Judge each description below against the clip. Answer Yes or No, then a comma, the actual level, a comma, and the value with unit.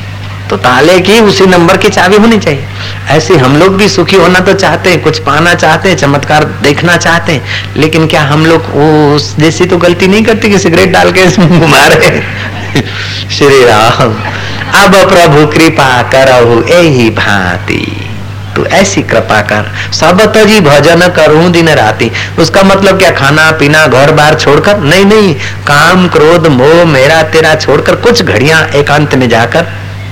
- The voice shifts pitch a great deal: Yes, wide, 8.1 semitones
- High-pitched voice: No, medium, 150 Hz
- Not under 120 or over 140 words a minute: No, average, 160 wpm